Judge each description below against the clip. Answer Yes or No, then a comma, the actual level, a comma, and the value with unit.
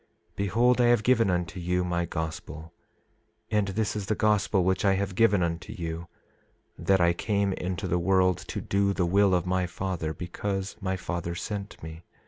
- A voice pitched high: No, very low, 95 Hz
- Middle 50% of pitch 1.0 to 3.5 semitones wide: Yes, narrow, 2.6 semitones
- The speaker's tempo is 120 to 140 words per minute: No, average, 180 wpm